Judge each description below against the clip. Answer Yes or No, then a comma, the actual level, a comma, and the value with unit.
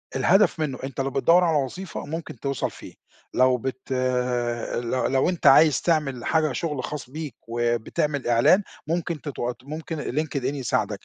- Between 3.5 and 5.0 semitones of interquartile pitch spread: Yes, average, 3.8 semitones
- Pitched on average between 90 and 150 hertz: Yes, low, 135 Hz